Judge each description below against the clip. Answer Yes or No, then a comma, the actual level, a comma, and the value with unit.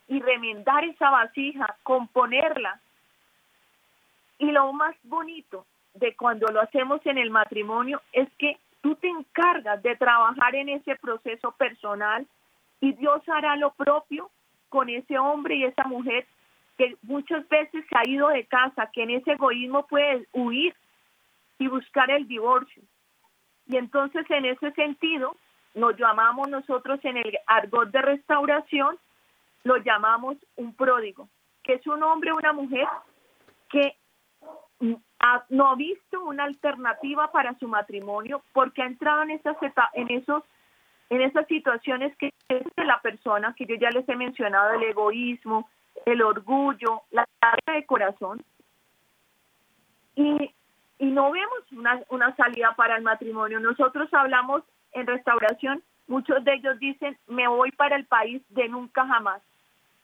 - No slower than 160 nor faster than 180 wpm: No, average, 145 wpm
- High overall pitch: Yes, very high, 260 Hz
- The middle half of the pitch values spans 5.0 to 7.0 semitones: No, average, 3.3 semitones